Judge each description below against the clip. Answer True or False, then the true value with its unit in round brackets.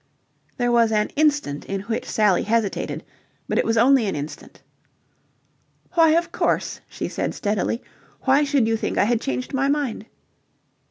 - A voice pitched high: True (230 Hz)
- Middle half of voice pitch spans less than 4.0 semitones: False (4.6 semitones)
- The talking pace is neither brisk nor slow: True (160 wpm)